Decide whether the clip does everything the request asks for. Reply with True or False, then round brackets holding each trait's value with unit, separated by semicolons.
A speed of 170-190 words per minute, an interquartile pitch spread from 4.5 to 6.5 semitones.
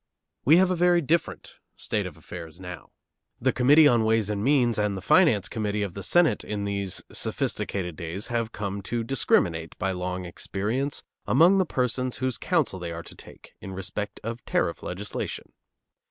True (175 wpm; 5.5 semitones)